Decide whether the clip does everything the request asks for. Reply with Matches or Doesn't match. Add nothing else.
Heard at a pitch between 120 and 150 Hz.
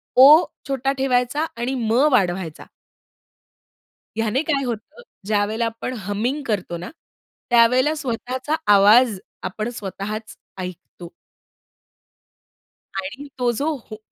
Doesn't match